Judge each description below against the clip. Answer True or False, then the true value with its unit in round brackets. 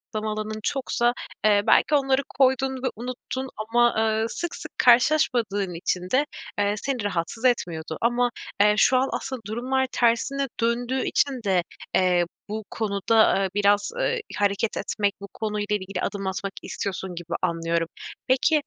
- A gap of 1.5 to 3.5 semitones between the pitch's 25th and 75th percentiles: False (4.3 semitones)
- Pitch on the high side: True (220 Hz)